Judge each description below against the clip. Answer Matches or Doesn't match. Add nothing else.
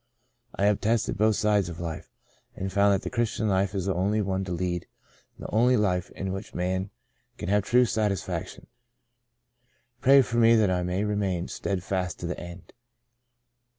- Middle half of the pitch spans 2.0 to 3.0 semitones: Matches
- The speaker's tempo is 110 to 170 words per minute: Doesn't match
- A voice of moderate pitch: Doesn't match